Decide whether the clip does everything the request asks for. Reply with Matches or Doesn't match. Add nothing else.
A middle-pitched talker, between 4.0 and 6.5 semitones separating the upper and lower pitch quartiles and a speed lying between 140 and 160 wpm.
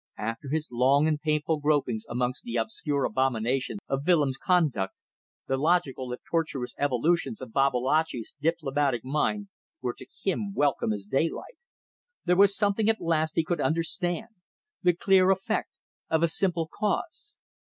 Matches